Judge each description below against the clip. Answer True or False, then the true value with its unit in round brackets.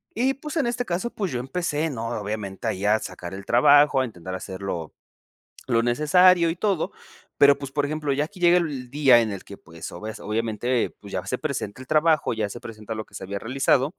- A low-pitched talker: True (130 Hz)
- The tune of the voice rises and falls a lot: True (6.8 semitones)